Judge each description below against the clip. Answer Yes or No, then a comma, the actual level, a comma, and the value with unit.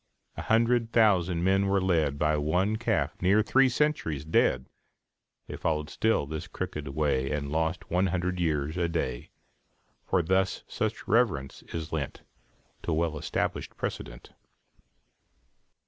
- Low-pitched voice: Yes, very low, 85 Hz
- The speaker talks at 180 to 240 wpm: No, slow, 135 wpm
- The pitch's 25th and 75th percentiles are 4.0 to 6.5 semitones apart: Yes, average, 4.3 semitones